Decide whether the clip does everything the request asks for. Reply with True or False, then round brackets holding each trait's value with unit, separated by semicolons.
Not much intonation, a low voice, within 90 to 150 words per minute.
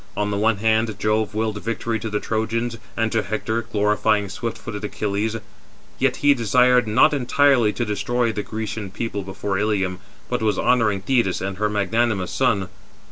False (2.1 semitones; 110 Hz; 170 wpm)